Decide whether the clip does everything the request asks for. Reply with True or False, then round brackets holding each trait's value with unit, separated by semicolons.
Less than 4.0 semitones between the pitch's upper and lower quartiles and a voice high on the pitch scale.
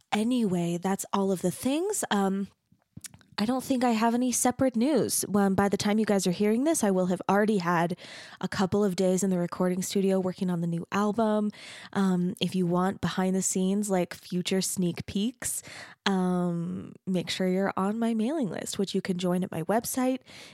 True (2.8 semitones; 195 Hz)